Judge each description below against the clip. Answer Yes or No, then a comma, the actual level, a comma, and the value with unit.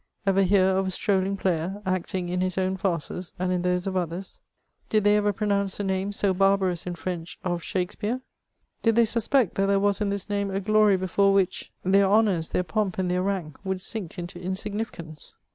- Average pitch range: No, narrow, 1.9 semitones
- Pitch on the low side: No, high, 190 Hz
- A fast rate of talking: Yes, fast, 210 wpm